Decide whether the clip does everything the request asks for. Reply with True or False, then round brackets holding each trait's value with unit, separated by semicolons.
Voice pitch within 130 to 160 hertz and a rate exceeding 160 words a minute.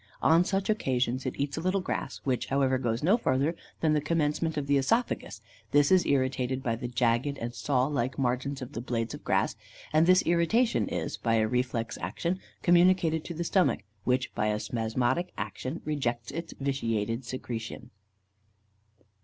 True (135 Hz; 170 wpm)